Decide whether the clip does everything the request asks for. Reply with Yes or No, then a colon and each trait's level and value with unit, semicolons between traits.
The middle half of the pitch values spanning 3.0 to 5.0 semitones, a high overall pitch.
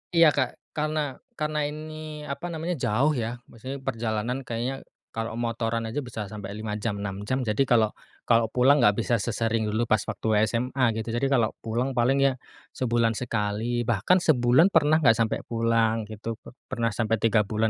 No: average, 3.3 semitones; low, 120 Hz